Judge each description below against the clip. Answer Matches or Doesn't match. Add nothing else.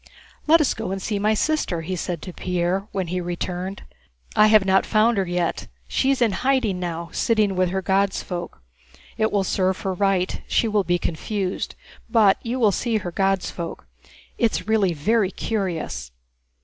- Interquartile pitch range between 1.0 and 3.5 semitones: Matches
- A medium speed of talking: Matches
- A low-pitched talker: Doesn't match